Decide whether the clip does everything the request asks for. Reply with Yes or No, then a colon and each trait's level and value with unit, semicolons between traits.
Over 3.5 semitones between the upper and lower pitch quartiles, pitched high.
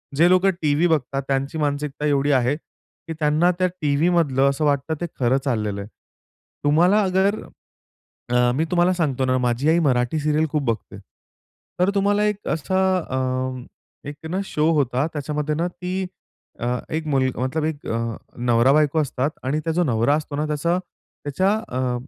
No: average, 4.2 semitones; medium, 150 Hz